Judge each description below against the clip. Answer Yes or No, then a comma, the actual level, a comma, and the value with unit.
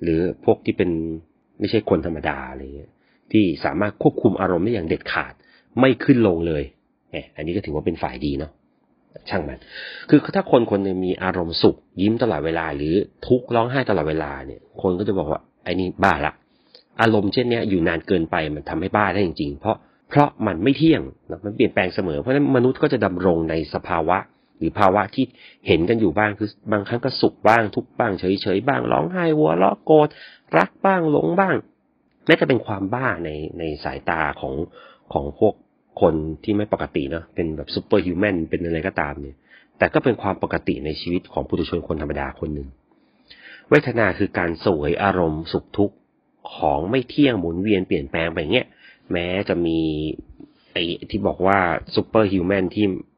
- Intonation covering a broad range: Yes, wide, 6.1 semitones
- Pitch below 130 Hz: Yes, very low, 95 Hz